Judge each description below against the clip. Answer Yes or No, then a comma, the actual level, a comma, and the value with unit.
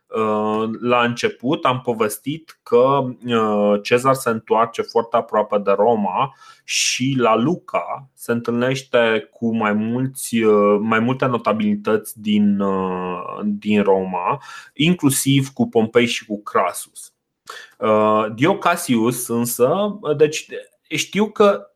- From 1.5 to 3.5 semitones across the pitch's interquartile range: No, average, 4.6 semitones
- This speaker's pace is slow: Yes, slow, 100 wpm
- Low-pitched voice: Yes, low, 120 Hz